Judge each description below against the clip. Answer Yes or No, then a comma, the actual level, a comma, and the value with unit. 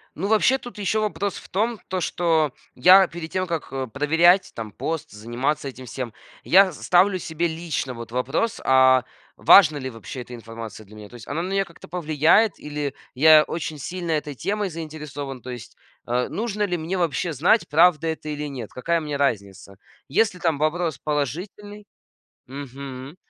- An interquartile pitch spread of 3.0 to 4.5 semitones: No, wide, 5.4 semitones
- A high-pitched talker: No, medium, 155 Hz